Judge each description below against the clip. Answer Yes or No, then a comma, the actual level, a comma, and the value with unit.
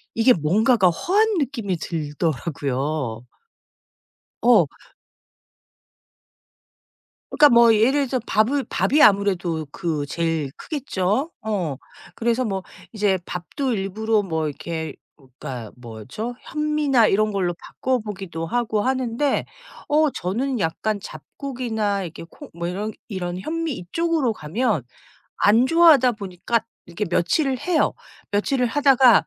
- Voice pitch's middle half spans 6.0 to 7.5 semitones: Yes, wide, 7.0 semitones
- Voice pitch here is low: No, high, 210 Hz